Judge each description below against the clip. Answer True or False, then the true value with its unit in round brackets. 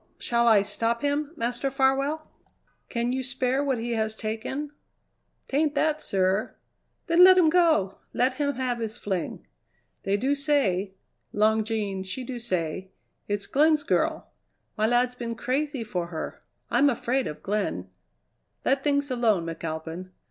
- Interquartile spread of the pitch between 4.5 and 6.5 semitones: True (5.5 semitones)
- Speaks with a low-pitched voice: False (240 Hz)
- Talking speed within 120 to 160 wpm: True (150 wpm)